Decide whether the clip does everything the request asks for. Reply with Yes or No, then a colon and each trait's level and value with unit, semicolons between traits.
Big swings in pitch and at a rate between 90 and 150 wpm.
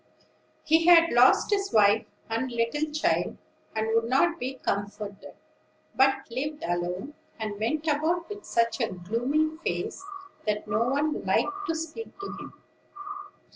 Yes: wide, 6.4 semitones; average, 140 wpm